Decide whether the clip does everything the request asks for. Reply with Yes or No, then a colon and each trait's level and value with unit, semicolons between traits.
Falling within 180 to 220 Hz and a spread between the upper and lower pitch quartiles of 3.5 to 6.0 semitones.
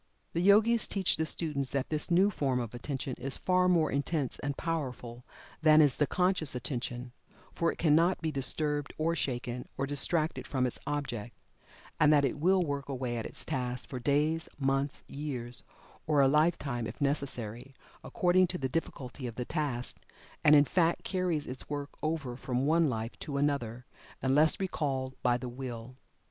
No: medium, 140 Hz; average, 4.0 semitones